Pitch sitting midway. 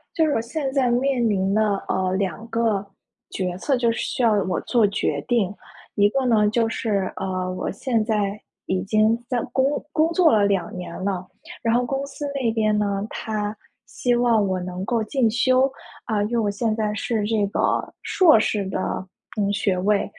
No: high, 215 Hz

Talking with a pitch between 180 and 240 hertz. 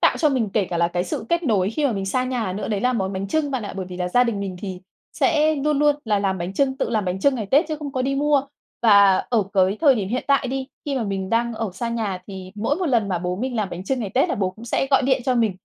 Yes: high, 225 Hz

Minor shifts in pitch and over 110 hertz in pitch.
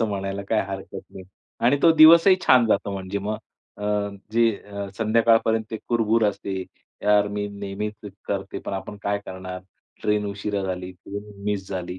No: narrow, 2.2 semitones; low, 105 Hz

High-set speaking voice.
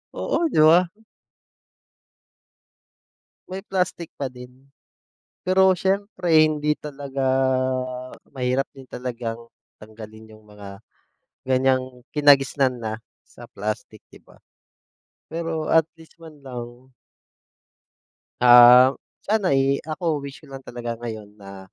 No: low, 135 Hz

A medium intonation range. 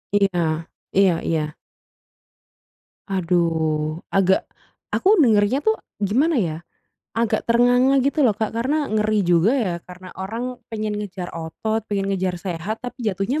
Yes: average, 4.8 semitones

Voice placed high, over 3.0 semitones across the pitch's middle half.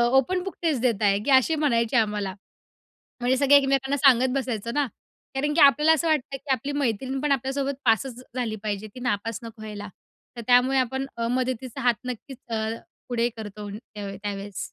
Yes: very high, 250 Hz; average, 3.6 semitones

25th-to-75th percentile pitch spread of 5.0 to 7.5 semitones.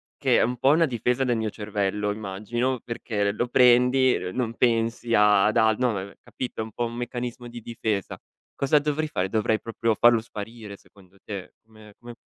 No: average, 2.8 semitones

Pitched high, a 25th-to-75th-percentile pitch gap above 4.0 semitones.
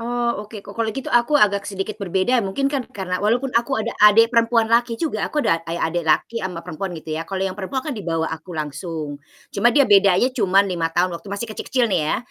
Yes: high, 200 Hz; average, 4.9 semitones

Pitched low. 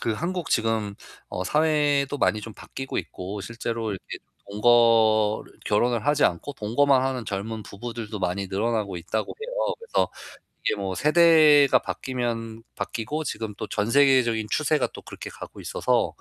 Yes: low, 115 Hz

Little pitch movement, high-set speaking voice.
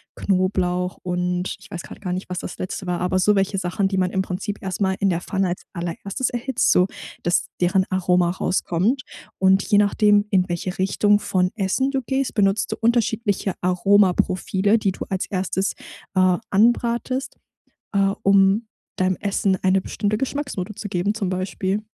Yes: narrow, 2.1 semitones; high, 195 Hz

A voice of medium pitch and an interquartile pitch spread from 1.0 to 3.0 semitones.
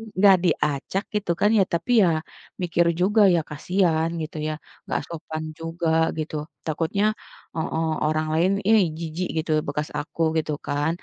Yes: medium, 165 Hz; narrow, 2.6 semitones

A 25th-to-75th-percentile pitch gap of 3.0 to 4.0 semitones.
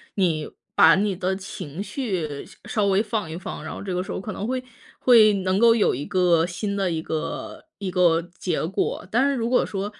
Yes: average, 3.4 semitones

